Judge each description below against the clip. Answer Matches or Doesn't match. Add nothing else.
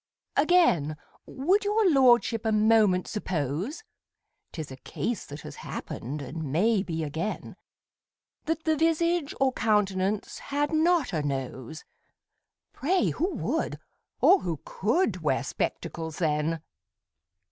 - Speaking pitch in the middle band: Doesn't match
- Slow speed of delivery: Matches